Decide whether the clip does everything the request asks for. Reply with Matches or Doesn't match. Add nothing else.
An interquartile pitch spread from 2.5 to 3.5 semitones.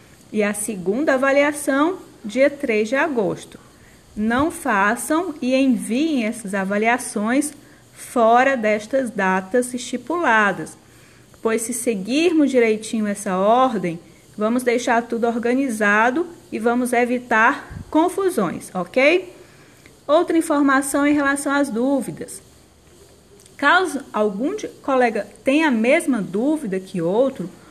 Doesn't match